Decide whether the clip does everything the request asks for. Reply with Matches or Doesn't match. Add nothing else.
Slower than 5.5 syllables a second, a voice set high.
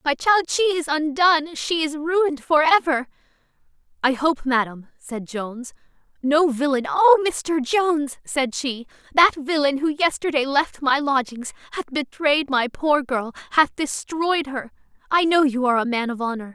Matches